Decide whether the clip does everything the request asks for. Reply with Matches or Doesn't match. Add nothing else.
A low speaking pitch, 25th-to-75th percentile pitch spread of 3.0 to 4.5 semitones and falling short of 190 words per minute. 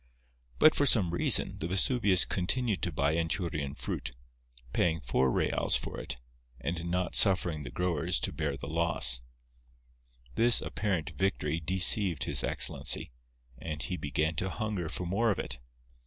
Matches